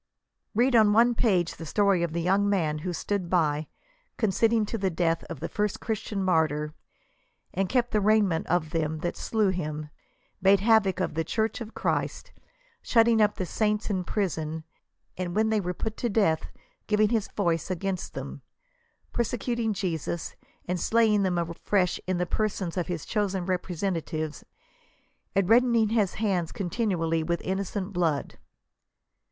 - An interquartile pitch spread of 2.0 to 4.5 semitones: Yes, average, 4.0 semitones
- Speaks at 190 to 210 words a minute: No, average, 160 wpm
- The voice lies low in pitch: No, high, 190 Hz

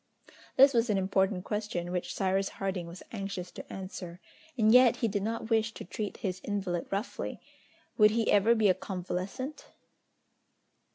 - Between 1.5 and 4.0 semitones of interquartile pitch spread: Yes, average, 3.0 semitones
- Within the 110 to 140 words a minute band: No, average, 160 wpm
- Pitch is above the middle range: Yes, high, 200 Hz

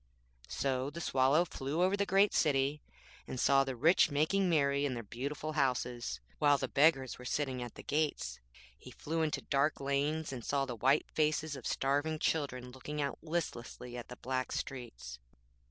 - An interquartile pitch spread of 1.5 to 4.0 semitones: Yes, average, 3.3 semitones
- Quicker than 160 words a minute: Yes, average, 175 wpm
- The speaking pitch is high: No, medium, 140 Hz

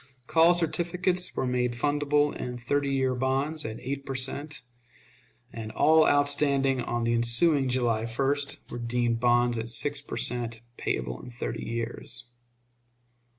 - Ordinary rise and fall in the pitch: Yes, average, 3.4 semitones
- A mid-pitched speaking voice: No, low, 130 Hz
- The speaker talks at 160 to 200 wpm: No, average, 145 wpm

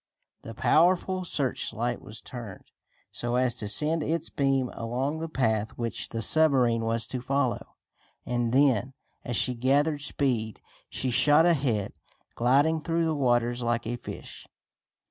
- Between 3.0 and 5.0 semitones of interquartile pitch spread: Yes, average, 3.9 semitones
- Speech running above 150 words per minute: No, average, 145 wpm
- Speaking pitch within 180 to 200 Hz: No, low, 125 Hz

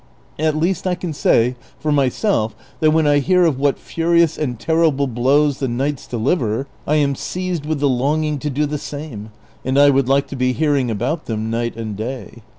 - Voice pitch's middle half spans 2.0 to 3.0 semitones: No, average, 3.6 semitones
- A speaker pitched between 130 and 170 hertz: Yes, medium, 140 Hz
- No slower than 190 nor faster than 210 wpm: Yes, average, 200 wpm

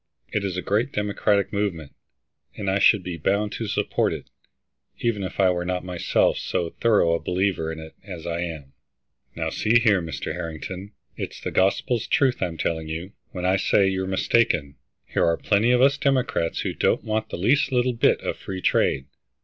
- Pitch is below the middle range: Yes, very low, 95 Hz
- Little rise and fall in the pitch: No, average, 3.9 semitones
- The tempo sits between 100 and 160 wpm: No, average, 190 wpm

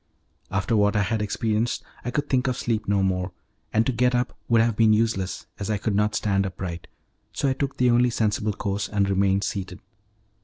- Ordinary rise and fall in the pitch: Yes, average, 3.0 semitones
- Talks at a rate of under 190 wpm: No, fast, 205 wpm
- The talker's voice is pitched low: Yes, low, 105 Hz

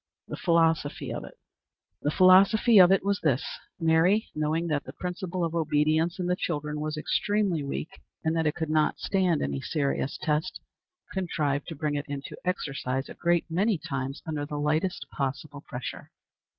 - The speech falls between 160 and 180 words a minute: Yes, average, 170 wpm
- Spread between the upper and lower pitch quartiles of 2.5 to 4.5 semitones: Yes, average, 3.4 semitones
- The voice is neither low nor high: Yes, medium, 160 Hz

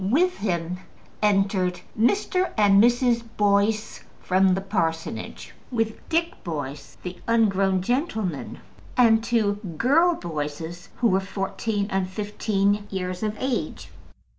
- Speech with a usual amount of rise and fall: Yes, average, 3.9 semitones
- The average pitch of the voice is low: No, high, 205 Hz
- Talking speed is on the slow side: Yes, slow, 115 wpm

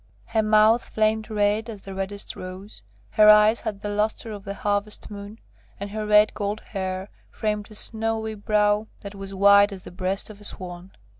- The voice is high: Yes, high, 210 Hz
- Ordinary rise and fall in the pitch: No, narrow, 1.4 semitones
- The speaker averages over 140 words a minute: Yes, average, 190 wpm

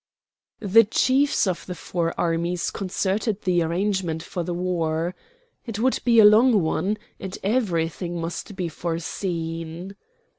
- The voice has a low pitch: No, medium, 180 Hz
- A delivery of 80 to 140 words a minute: Yes, slow, 135 wpm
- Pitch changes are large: No, average, 3.7 semitones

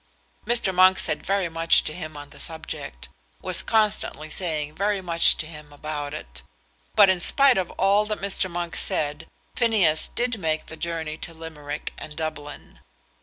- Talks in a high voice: No, medium, 165 Hz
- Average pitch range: Yes, average, 3.9 semitones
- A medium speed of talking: Yes, average, 170 wpm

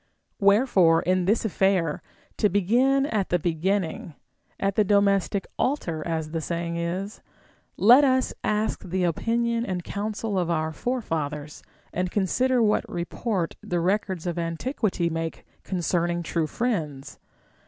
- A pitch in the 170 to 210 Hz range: Yes, medium, 185 Hz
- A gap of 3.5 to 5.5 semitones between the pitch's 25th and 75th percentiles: Yes, average, 4.2 semitones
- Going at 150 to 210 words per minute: No, average, 140 wpm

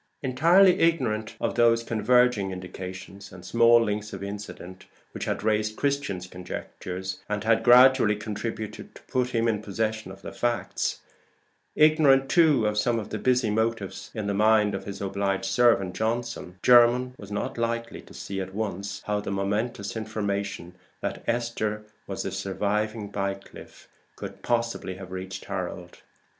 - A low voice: Yes, low, 105 Hz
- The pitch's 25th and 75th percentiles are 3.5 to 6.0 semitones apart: No, average, 3.1 semitones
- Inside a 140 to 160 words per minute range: Yes, average, 150 wpm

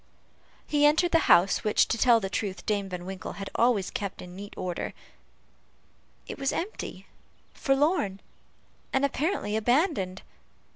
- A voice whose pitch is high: Yes, high, 215 Hz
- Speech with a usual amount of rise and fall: No, wide, 7.0 semitones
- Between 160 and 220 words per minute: No, average, 140 wpm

